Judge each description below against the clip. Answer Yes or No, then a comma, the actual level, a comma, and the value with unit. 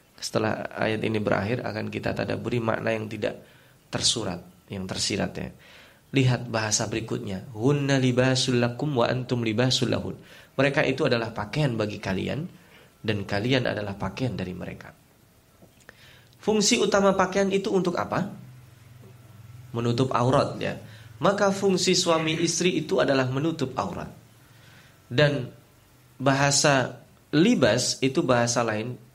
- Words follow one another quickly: No, average, 110 wpm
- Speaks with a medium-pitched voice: No, low, 125 Hz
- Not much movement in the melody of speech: No, average, 4.0 semitones